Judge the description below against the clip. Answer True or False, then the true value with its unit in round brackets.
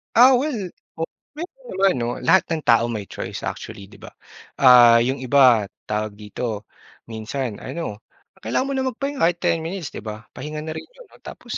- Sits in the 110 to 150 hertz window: True (140 Hz)